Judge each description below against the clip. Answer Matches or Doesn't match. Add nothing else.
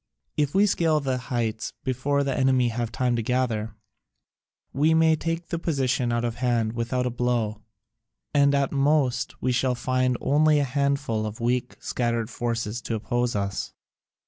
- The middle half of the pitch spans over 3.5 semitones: Doesn't match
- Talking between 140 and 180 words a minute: Matches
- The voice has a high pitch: Doesn't match